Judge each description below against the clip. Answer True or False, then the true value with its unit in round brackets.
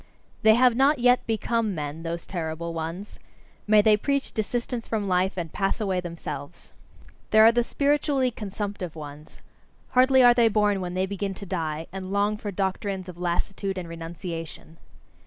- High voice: True (195 Hz)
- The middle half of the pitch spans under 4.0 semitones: False (4.6 semitones)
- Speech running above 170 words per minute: False (165 wpm)